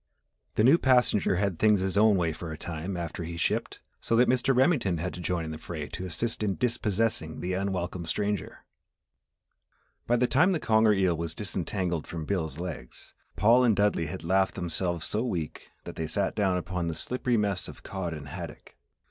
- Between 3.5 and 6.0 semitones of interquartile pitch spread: Yes, average, 4.5 semitones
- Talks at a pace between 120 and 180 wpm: No, average, 195 wpm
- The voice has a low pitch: Yes, very low, 95 Hz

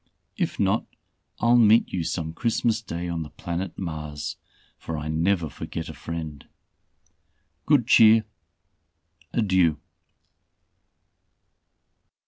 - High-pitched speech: No, very low, 85 Hz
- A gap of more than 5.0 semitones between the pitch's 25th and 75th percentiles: Yes, wide, 5.5 semitones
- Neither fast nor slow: No, slow, 105 wpm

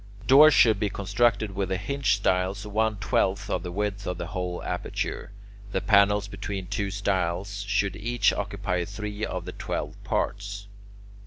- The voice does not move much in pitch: Yes, narrow, 1.7 semitones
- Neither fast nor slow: Yes, average, 160 wpm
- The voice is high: No, low, 100 Hz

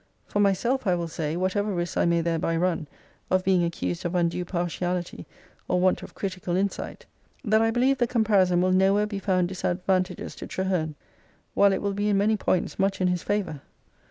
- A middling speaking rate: Yes, average, 195 wpm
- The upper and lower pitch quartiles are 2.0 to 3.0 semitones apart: Yes, narrow, 2.5 semitones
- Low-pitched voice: No, medium, 185 Hz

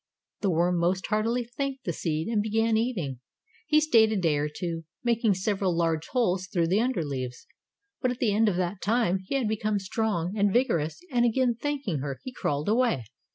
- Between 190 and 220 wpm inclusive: Yes, average, 200 wpm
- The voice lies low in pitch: No, high, 205 Hz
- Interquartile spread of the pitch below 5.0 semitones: No, wide, 5.6 semitones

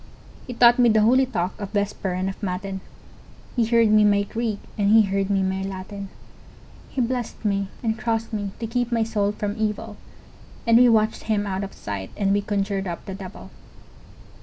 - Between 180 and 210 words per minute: Yes, average, 195 wpm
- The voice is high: Yes, high, 205 Hz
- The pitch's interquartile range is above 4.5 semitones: No, narrow, 2.5 semitones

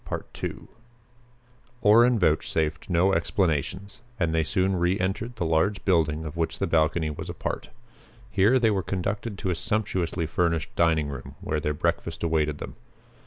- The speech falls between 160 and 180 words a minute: No, average, 150 wpm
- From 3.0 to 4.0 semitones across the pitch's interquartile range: Yes, average, 3.5 semitones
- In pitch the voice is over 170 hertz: No, very low, 85 Hz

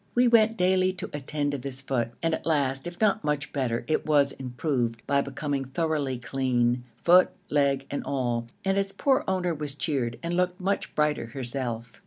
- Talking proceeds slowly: No, average, 185 wpm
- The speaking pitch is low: No, medium, 145 Hz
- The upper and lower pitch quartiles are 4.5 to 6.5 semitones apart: Yes, average, 5.0 semitones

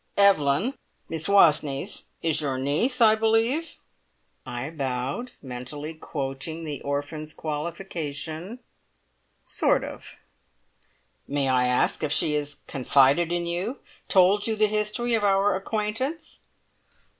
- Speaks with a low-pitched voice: No, medium, 160 Hz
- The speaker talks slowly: Yes, slow, 115 wpm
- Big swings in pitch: Yes, wide, 6.6 semitones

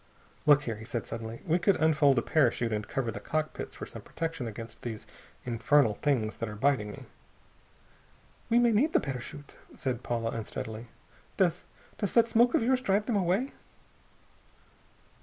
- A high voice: No, low, 135 Hz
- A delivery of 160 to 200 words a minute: Yes, average, 165 wpm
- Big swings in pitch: Yes, wide, 7.8 semitones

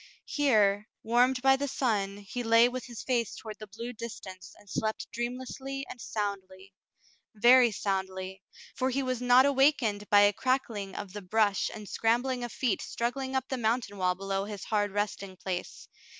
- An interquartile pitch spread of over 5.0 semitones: No, average, 4.0 semitones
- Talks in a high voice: Yes, high, 225 Hz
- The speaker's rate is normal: Yes, average, 175 wpm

